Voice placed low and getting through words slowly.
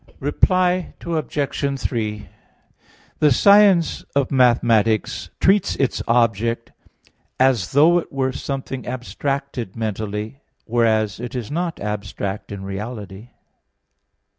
Yes: low, 120 Hz; slow, 100 wpm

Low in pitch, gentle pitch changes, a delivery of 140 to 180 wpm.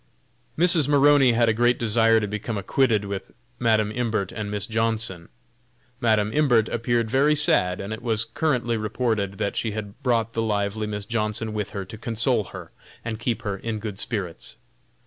Yes: low, 110 Hz; narrow, 2.3 semitones; average, 175 wpm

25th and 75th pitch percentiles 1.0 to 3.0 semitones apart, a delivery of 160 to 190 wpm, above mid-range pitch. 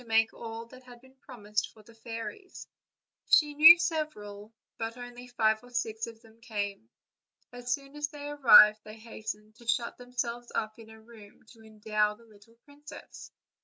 Yes: narrow, 2.4 semitones; average, 170 wpm; high, 230 Hz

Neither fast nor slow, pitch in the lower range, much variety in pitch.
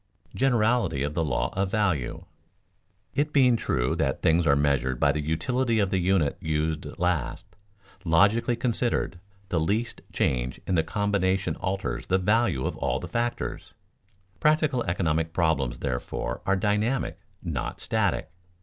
Yes: average, 145 wpm; very low, 95 Hz; wide, 6.3 semitones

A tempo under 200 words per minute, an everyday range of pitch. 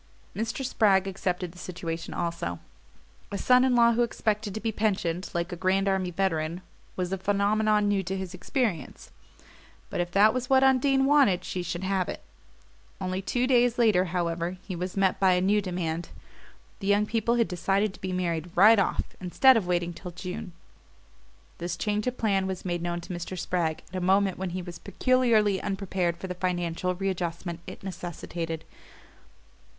Yes: average, 180 wpm; average, 3.1 semitones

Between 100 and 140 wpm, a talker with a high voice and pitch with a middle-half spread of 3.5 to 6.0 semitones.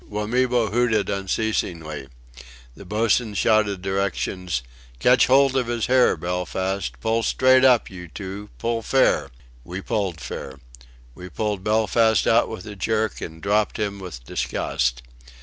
No: slow, 135 wpm; low, 105 Hz; average, 3.8 semitones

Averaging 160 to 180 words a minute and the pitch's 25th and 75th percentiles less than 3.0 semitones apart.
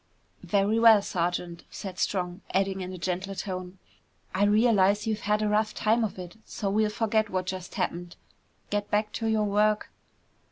Yes: average, 170 wpm; narrow, 2.5 semitones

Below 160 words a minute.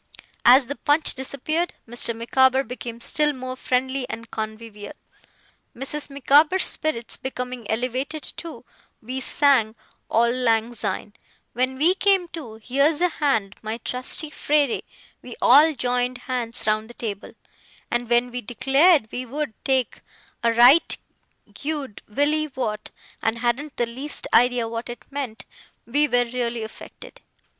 Yes: average, 140 wpm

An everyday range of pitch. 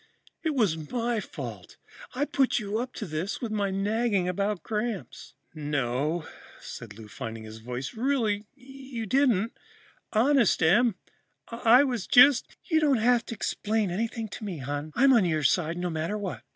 No: wide, 6.8 semitones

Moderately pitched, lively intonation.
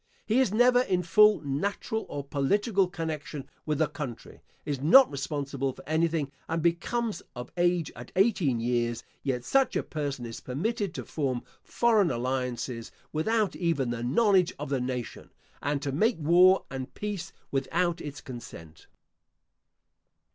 Yes: medium, 150 Hz; wide, 6.4 semitones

